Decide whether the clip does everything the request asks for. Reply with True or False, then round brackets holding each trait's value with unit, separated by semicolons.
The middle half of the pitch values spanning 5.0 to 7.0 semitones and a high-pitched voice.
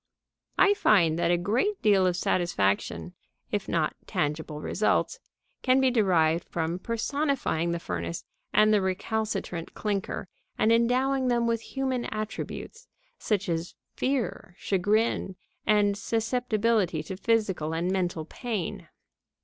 True (5.3 semitones; 205 Hz)